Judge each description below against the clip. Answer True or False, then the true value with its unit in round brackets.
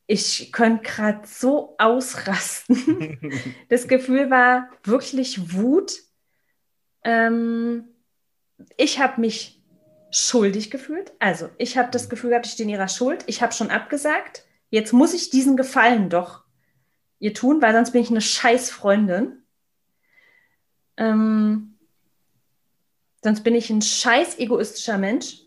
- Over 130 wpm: False (125 wpm)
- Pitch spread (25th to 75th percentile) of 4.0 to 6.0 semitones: False (3.4 semitones)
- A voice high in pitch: True (235 Hz)